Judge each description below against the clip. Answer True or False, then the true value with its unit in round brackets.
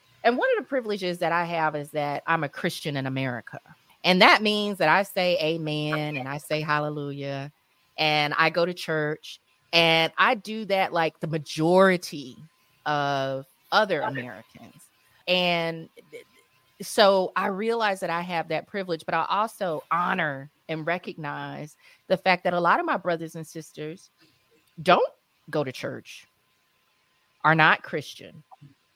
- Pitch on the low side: False (165 Hz)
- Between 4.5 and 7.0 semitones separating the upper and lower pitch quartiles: False (3.7 semitones)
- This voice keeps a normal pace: True (150 wpm)